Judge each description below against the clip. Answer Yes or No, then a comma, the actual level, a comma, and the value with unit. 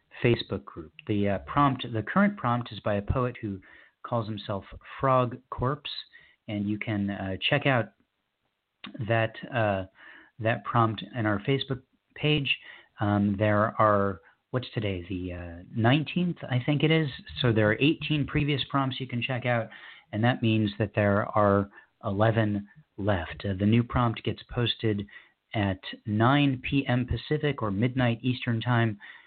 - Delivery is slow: No, average, 155 wpm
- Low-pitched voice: Yes, low, 115 Hz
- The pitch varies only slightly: No, average, 3.8 semitones